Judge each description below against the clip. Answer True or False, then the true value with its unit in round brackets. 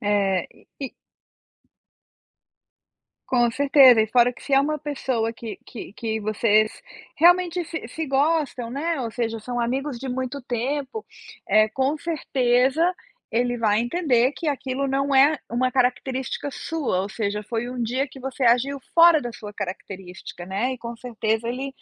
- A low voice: False (250 Hz)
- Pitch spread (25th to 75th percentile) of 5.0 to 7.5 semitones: False (3.4 semitones)